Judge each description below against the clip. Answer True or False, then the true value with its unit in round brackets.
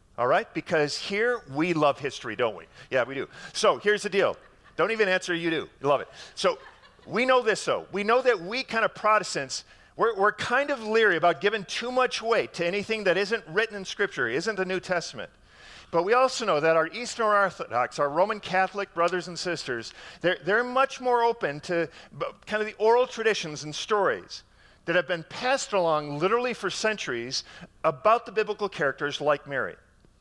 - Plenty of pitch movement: False (5.0 semitones)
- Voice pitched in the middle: False (200 Hz)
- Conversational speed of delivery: True (195 wpm)